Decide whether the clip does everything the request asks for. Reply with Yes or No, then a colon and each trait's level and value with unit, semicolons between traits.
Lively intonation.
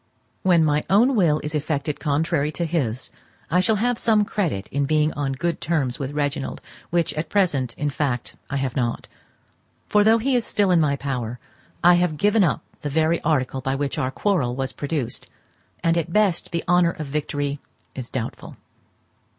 No: average, 4.2 semitones